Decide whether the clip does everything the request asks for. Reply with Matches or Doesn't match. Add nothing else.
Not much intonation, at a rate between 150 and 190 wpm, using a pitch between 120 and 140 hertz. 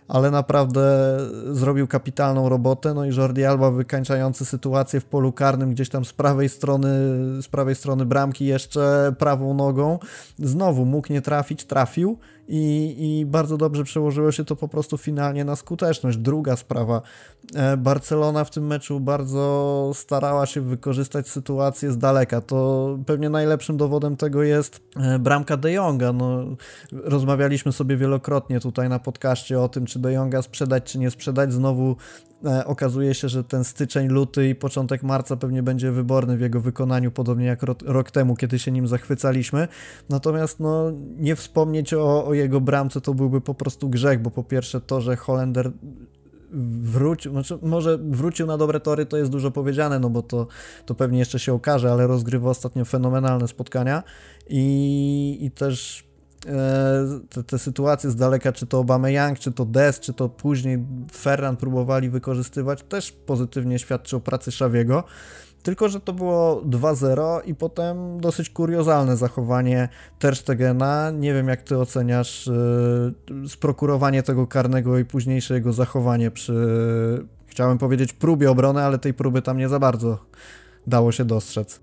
Matches